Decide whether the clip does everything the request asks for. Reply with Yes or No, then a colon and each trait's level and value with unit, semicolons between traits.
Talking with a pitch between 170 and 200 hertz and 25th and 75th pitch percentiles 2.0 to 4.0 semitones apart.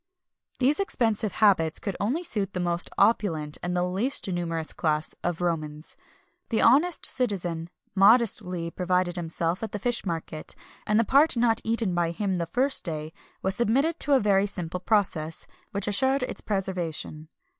No: high, 190 Hz; average, 5.2 semitones